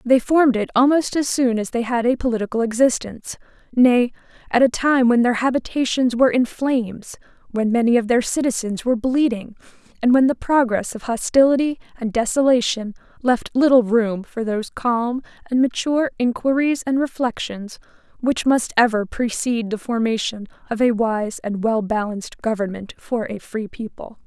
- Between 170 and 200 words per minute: No, average, 160 wpm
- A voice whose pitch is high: Yes, high, 240 Hz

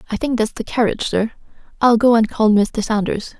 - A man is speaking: No, female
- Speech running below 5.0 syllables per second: No, 5.6 syllables/s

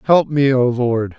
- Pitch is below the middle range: Yes, low, 130 Hz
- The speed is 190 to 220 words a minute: Yes, fast, 205 wpm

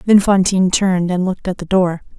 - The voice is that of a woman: Yes, female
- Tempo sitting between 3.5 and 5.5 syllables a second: No, 6.2 syllables/s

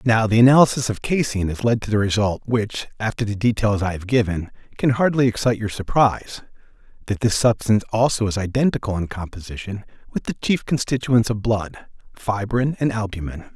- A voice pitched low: Yes, low, 110 Hz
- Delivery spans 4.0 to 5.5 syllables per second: No, 5.8 syllables/s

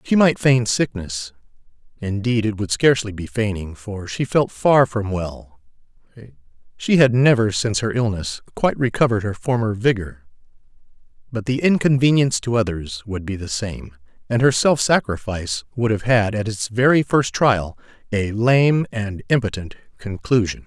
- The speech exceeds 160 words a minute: No, average, 150 wpm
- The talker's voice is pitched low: Yes, low, 110 Hz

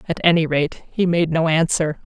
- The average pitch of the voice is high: No, medium, 165 Hz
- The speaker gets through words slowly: No, average, 200 wpm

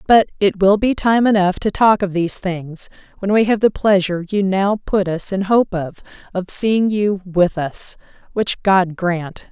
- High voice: Yes, high, 195 Hz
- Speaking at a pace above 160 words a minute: Yes, average, 195 wpm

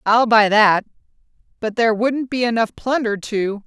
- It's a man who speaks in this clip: No, female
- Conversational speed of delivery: Yes, average, 165 wpm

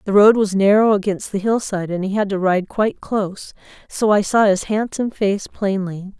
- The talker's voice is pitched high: Yes, high, 200 Hz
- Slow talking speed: No, fast, 205 wpm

